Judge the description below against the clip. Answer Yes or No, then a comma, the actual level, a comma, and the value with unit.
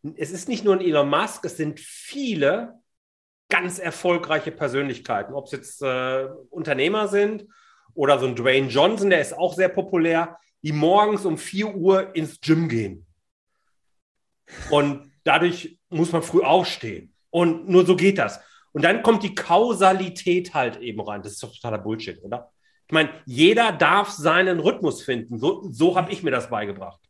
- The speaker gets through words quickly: No, average, 170 wpm